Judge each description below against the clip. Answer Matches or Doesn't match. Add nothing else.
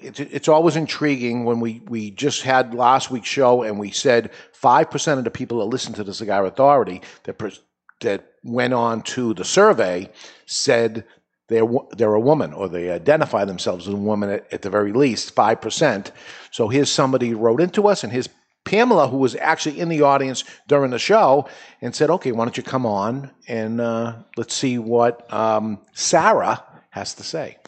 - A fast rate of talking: Doesn't match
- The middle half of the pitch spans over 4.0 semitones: Doesn't match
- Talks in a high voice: Doesn't match